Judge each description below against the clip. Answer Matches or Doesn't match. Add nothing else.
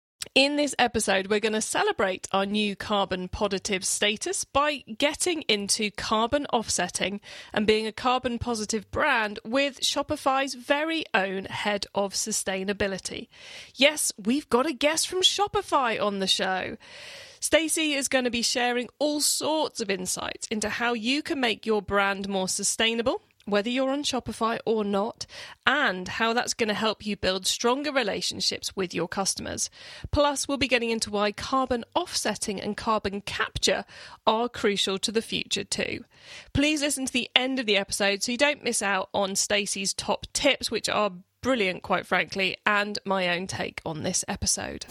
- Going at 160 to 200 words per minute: Matches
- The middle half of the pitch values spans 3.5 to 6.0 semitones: Matches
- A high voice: Matches